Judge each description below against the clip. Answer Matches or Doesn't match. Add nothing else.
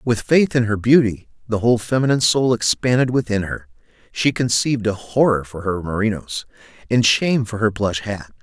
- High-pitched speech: Doesn't match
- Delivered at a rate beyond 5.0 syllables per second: Matches